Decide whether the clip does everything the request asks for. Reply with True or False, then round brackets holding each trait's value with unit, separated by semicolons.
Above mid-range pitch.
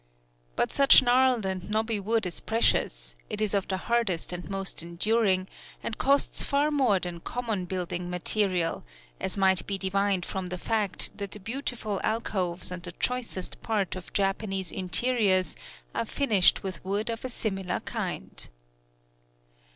True (195 Hz)